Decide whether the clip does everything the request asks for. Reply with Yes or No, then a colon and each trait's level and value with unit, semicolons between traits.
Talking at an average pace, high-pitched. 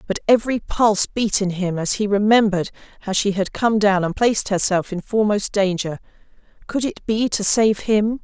Yes: average, 180 wpm; high, 205 Hz